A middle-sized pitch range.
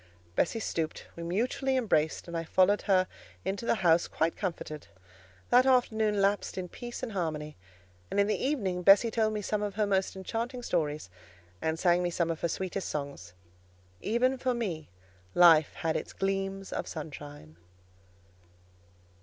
Yes: average, 4.8 semitones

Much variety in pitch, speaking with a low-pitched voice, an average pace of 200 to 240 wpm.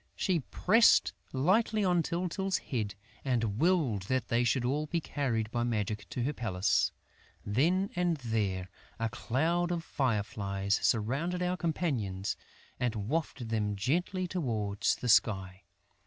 No: wide, 8.3 semitones; low, 125 Hz; slow, 135 wpm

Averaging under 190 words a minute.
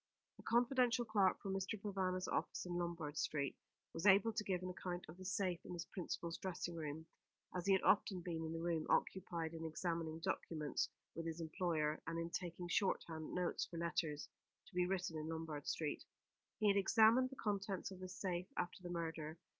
No: average, 195 wpm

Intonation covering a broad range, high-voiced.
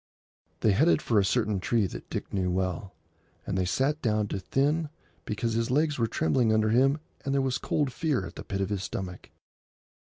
No: wide, 5.8 semitones; low, 110 Hz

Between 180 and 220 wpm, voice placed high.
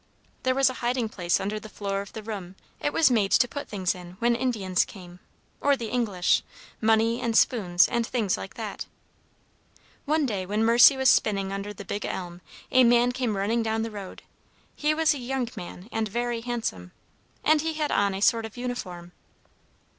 Yes: average, 190 wpm; high, 225 Hz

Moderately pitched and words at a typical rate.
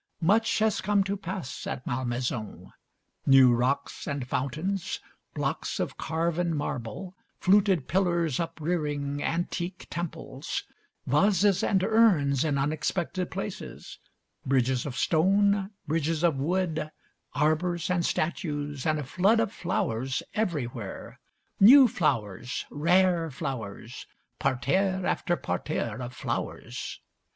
No: medium, 160 Hz; slow, 110 wpm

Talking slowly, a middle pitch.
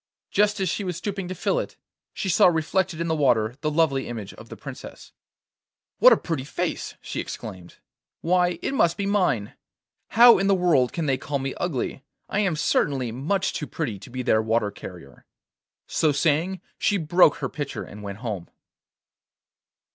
No: average, 180 wpm; medium, 155 Hz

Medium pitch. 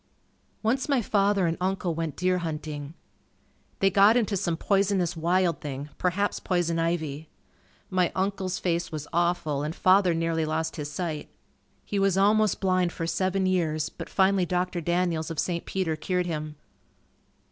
Yes: medium, 175 Hz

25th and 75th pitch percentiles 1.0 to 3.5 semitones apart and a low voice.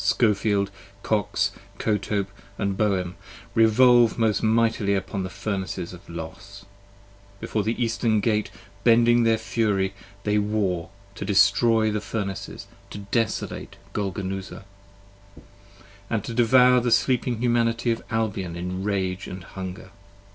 Yes: average, 2.9 semitones; low, 105 Hz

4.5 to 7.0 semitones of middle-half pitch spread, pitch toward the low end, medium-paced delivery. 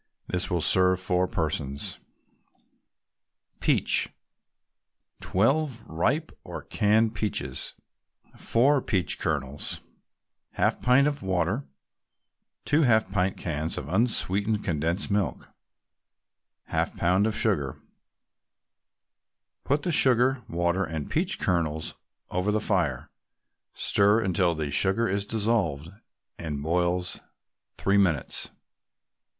No: average, 5.1 semitones; very low, 95 Hz; slow, 100 wpm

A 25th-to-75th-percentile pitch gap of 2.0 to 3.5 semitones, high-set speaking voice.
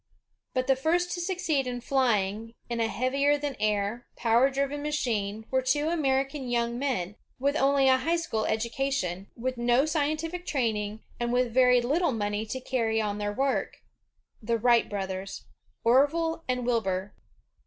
No: average, 4.0 semitones; very high, 250 Hz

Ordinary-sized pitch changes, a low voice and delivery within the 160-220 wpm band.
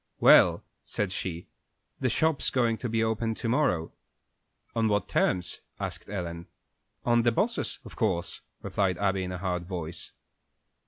No: average, 4.4 semitones; low, 100 Hz; average, 150 wpm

